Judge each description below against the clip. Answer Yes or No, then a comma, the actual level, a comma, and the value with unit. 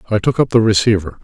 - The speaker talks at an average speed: No, fast, 245 wpm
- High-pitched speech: No, low, 110 Hz